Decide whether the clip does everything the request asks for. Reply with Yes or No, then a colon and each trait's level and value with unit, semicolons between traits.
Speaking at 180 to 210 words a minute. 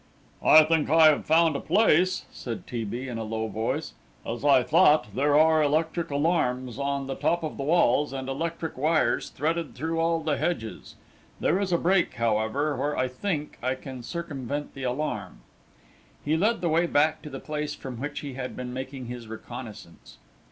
Yes: average, 185 wpm